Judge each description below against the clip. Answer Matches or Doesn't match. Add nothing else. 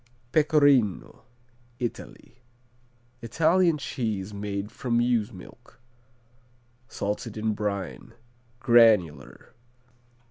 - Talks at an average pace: Doesn't match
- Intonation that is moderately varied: Matches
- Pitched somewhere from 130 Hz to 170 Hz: Doesn't match